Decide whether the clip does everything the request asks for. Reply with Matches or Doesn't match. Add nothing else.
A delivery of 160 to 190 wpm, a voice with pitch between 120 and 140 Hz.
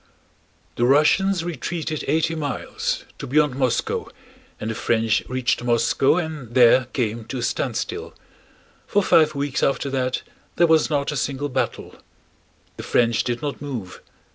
Doesn't match